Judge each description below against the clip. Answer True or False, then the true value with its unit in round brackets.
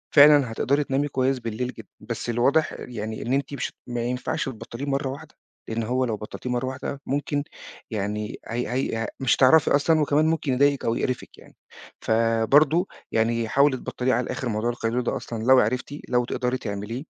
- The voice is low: True (125 Hz)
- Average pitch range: True (3.3 semitones)